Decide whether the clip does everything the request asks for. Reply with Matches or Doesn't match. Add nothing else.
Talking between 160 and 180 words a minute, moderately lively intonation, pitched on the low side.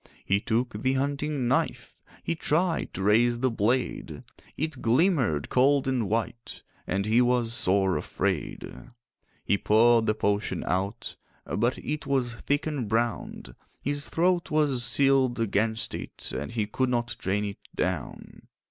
Doesn't match